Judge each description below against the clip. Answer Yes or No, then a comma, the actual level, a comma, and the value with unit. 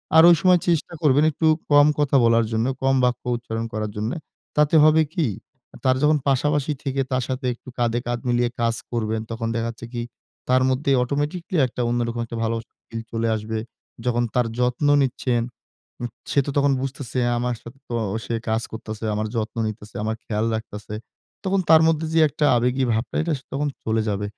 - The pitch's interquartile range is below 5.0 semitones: Yes, average, 4.0 semitones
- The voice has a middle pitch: No, low, 125 Hz